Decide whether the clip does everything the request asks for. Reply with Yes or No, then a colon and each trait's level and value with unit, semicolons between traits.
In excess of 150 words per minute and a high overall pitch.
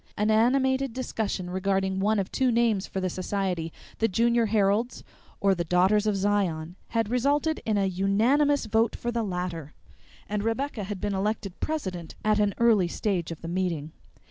Yes: average, 170 wpm; high, 205 Hz